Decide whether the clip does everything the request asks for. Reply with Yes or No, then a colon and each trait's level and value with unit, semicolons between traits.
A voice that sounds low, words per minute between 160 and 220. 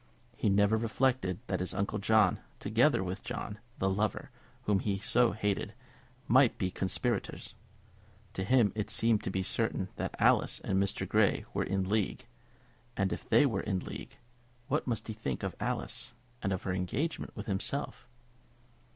Yes: low, 100 Hz; average, 170 wpm